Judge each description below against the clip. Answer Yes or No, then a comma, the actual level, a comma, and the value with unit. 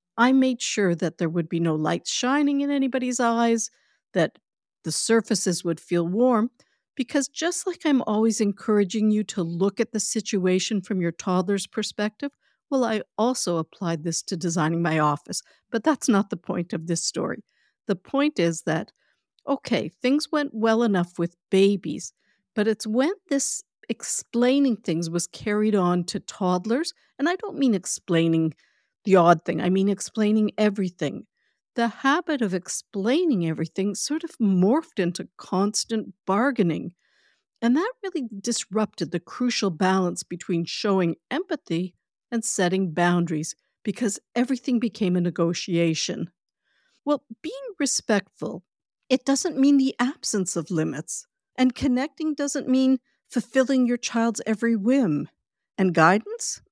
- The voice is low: No, high, 215 Hz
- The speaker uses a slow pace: No, average, 145 wpm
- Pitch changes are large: Yes, wide, 6.5 semitones